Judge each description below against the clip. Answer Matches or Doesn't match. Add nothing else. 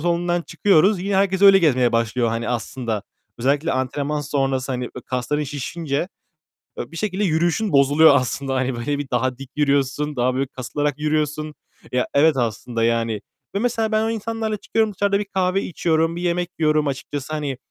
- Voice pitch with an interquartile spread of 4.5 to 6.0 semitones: Matches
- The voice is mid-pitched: Matches